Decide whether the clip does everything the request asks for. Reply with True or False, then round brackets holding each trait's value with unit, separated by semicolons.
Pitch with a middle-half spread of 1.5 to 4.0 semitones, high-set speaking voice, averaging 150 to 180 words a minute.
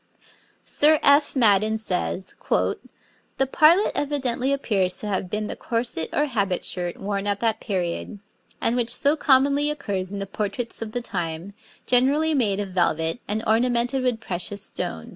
False (5.2 semitones; 220 Hz; 160 wpm)